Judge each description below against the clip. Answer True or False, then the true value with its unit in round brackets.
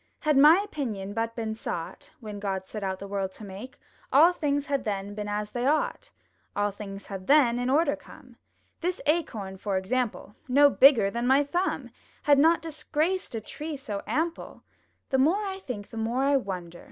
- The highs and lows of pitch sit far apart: True (6.4 semitones)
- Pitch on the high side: True (245 Hz)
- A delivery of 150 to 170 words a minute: False (190 wpm)